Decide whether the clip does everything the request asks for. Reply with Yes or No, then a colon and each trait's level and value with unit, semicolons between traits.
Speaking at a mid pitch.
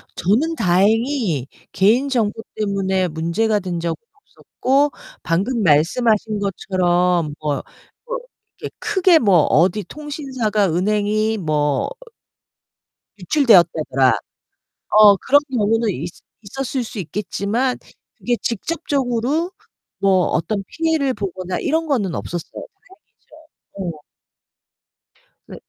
No: high, 210 Hz